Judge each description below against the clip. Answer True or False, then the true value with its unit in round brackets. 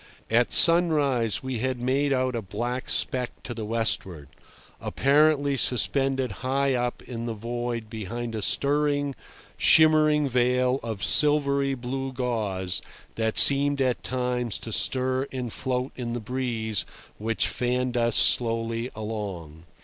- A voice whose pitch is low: True (125 Hz)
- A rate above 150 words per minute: False (135 wpm)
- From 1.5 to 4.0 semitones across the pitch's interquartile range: True (2.9 semitones)